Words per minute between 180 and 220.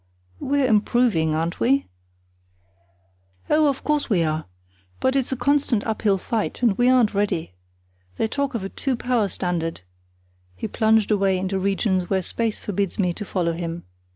No: average, 160 wpm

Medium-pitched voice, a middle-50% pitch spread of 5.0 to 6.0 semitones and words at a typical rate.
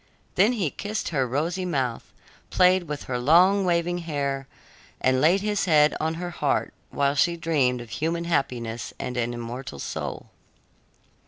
Yes: medium, 155 Hz; average, 5.3 semitones; average, 155 wpm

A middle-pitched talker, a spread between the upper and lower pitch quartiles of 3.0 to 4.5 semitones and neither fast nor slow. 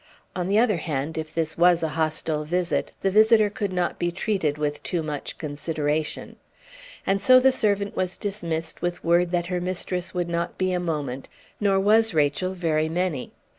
Yes: medium, 175 Hz; average, 3.5 semitones; average, 180 wpm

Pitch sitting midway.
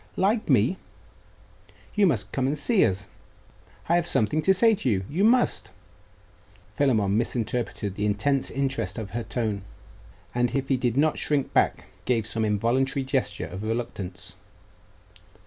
No: low, 125 Hz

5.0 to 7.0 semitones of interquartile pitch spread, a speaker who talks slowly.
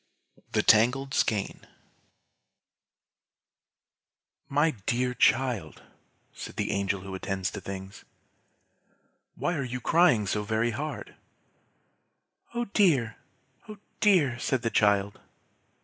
Yes: average, 5.3 semitones; slow, 105 wpm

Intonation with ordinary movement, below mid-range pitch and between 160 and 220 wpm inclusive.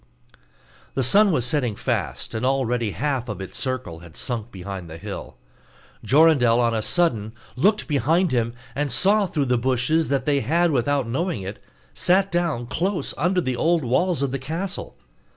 No: wide, 5.9 semitones; low, 130 Hz; average, 170 wpm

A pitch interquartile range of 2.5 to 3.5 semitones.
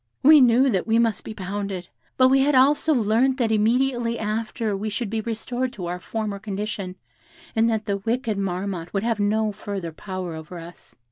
Yes: average, 3.2 semitones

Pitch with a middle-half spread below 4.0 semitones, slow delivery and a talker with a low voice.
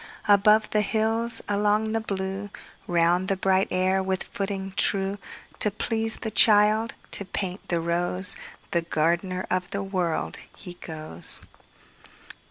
No: narrow, 2.5 semitones; slow, 120 wpm; high, 195 Hz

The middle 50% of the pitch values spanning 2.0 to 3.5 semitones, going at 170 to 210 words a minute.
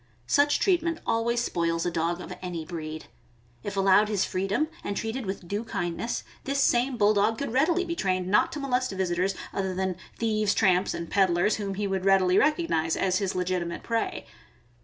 No: average, 4.5 semitones; average, 180 wpm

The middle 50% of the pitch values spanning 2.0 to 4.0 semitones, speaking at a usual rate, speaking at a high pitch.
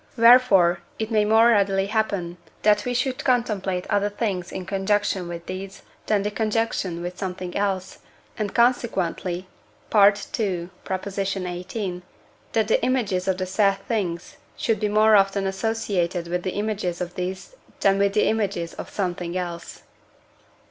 Yes: average, 3.0 semitones; average, 145 wpm; high, 195 Hz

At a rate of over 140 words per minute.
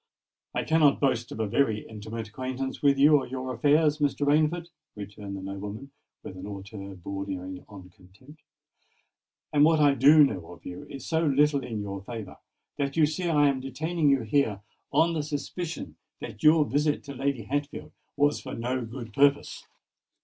Yes: average, 175 wpm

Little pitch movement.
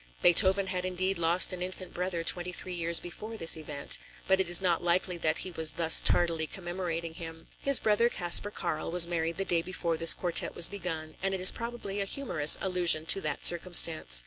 Yes: narrow, 2.3 semitones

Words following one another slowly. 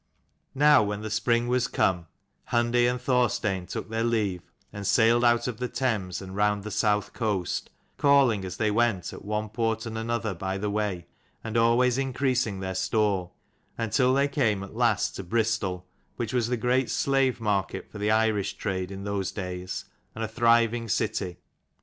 No: average, 175 wpm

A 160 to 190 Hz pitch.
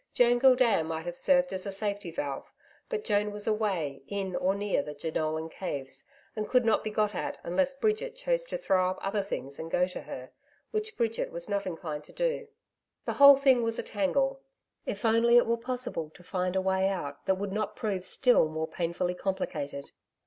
No: high, 200 Hz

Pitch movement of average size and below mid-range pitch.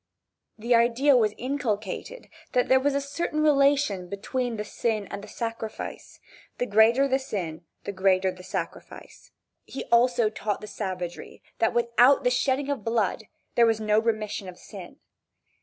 No: average, 4.0 semitones; high, 230 Hz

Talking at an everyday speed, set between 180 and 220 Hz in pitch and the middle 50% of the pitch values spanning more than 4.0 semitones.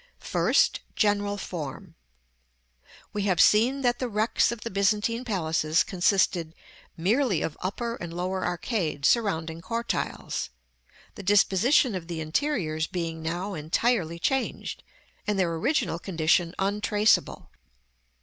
No: slow, 125 wpm; high, 190 Hz; average, 4.9 semitones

